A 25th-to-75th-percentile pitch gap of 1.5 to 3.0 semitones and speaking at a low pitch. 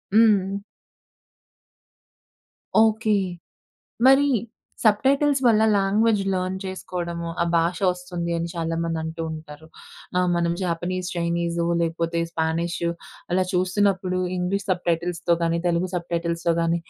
No: narrow, 2.4 semitones; medium, 175 Hz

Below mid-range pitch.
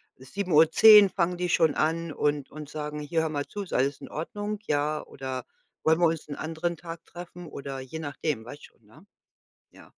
No: medium, 155 Hz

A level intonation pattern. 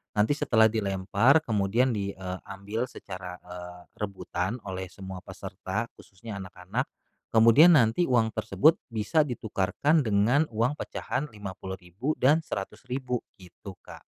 No: average, 4.8 semitones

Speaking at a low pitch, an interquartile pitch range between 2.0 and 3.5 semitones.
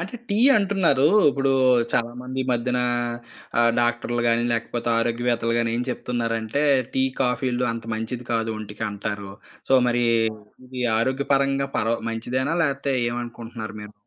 Yes: low, 120 Hz; narrow, 2.4 semitones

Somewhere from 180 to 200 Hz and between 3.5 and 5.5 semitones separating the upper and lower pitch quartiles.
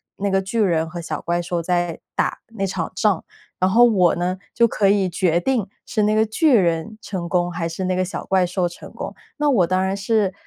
No: medium, 185 Hz; average, 2.9 semitones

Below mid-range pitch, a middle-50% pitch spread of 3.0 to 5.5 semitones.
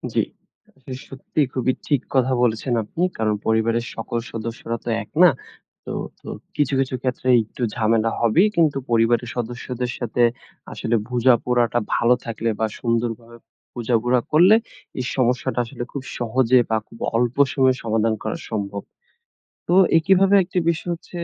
No: low, 120 Hz; narrow, 2.4 semitones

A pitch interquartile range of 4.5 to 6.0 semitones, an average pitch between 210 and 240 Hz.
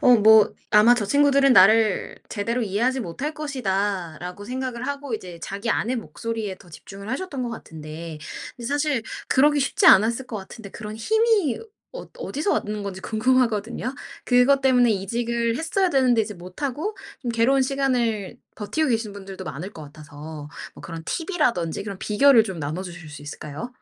Yes: average, 5.3 semitones; high, 225 Hz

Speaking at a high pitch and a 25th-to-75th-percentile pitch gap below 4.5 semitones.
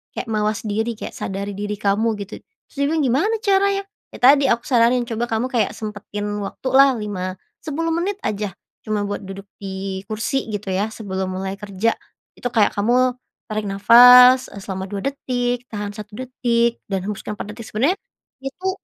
Yes: high, 220 Hz; average, 3.8 semitones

